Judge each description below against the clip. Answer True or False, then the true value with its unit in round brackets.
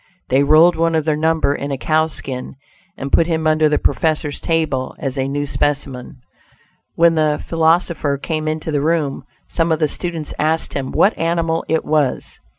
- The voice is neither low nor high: True (155 Hz)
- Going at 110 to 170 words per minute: False (180 wpm)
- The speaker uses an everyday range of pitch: False (2.3 semitones)